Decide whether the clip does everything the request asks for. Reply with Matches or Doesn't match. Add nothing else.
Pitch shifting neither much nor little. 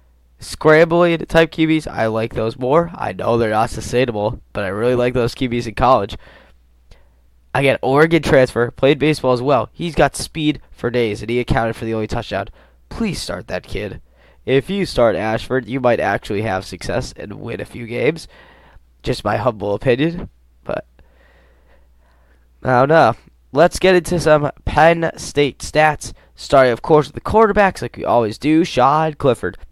Doesn't match